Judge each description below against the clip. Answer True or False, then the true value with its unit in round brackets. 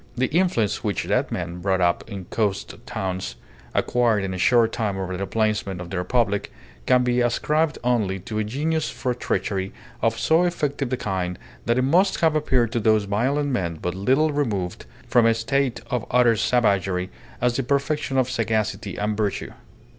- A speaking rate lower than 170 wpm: False (180 wpm)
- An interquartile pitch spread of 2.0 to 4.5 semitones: False (4.9 semitones)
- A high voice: False (115 Hz)